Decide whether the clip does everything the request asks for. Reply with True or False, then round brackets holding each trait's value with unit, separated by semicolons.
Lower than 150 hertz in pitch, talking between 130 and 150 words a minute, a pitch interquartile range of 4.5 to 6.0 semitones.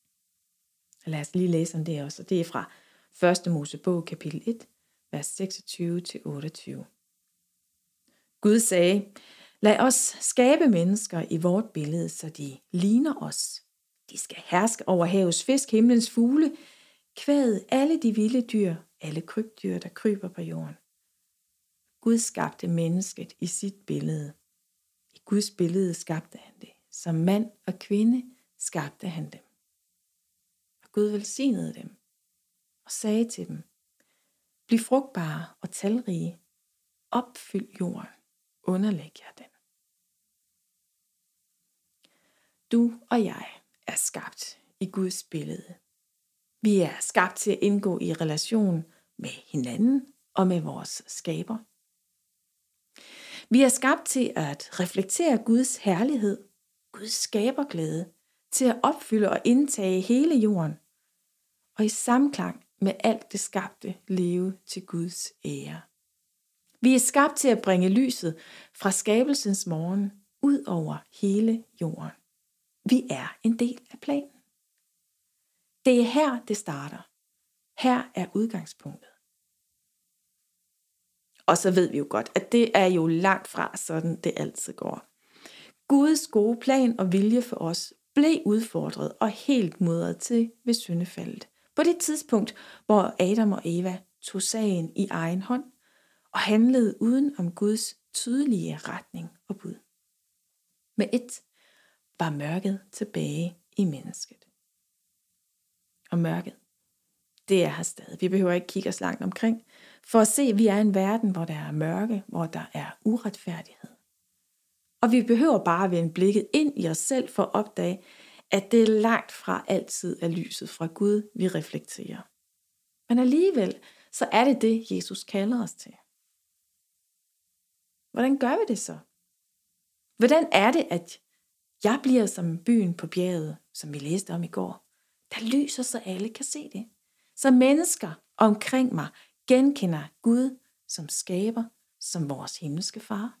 False (205 Hz; 135 wpm; 5.3 semitones)